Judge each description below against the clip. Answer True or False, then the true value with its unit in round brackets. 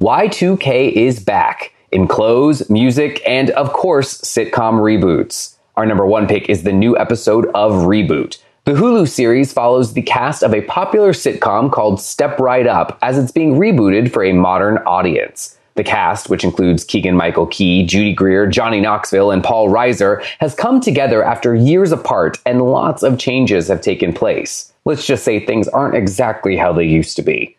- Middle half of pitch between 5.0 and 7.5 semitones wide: True (5.3 semitones)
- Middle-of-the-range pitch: False (115 Hz)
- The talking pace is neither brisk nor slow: True (175 wpm)